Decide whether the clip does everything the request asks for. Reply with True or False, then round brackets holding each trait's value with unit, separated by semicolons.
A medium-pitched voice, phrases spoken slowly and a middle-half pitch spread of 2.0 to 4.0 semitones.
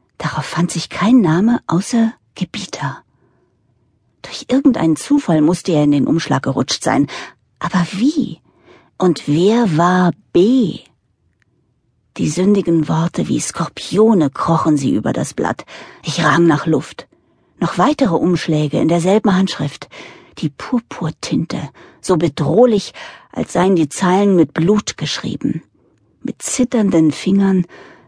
False (170 Hz; 120 wpm; 4.6 semitones)